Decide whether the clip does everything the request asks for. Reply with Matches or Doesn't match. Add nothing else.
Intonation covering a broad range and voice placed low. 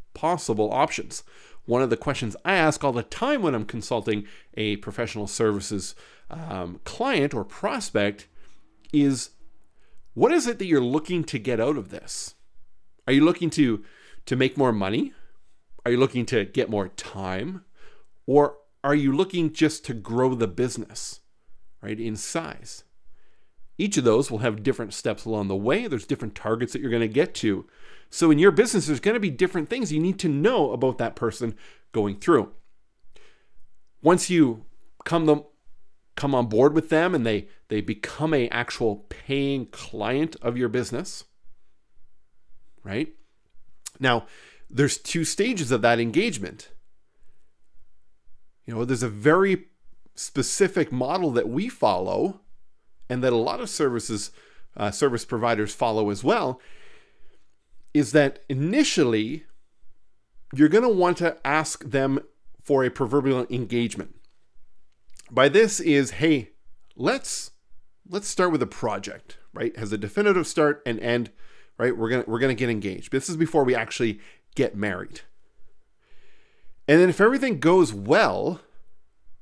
Matches